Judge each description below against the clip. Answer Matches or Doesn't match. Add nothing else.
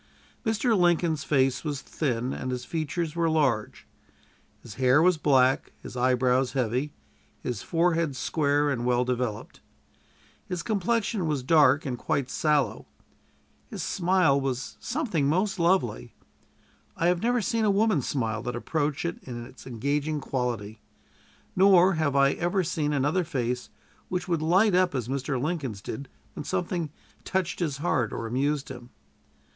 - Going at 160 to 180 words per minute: Doesn't match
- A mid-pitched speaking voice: Matches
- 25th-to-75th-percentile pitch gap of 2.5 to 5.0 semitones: Doesn't match